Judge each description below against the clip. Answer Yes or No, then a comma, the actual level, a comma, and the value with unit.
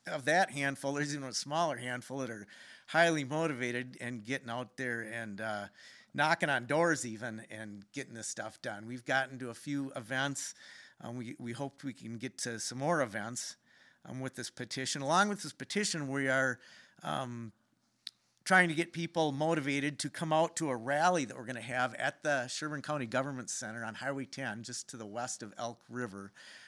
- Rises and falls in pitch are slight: No, average, 3.8 semitones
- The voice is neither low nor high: No, low, 130 Hz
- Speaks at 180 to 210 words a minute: Yes, average, 200 wpm